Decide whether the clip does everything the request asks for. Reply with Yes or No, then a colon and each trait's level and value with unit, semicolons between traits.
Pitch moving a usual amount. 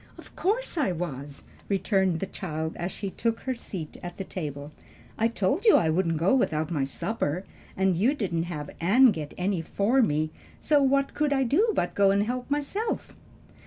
No: wide, 7.8 semitones